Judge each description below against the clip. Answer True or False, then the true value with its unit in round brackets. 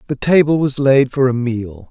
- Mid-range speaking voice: False (130 Hz)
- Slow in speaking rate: False (220 wpm)